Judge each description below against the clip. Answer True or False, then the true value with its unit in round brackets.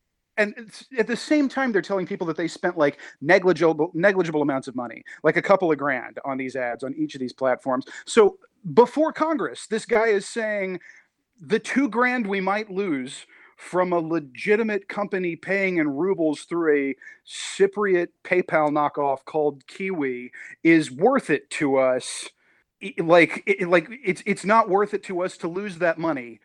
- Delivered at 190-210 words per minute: False (170 wpm)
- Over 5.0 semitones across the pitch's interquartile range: True (5.6 semitones)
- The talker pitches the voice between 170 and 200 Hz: True (185 Hz)